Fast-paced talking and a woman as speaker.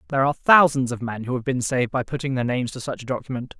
No: fast, 285 wpm; male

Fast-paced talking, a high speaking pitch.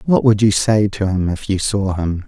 No: fast, 265 wpm; low, 100 Hz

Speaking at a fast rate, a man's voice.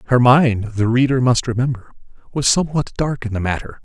No: average, 190 wpm; male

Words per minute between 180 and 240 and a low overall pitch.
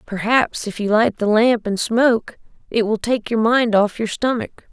No: fast, 205 wpm; high, 225 Hz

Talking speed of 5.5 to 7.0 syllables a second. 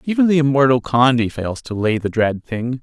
No: 5.1 syllables/s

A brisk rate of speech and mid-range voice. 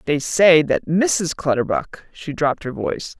No: average, 170 wpm; medium, 160 Hz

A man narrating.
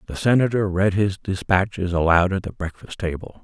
Yes: male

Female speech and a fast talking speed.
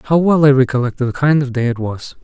No: male; fast, 270 wpm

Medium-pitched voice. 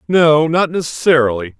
Yes: medium, 145 Hz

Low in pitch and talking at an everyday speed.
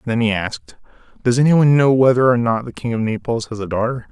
No: low, 115 Hz; fast, 250 wpm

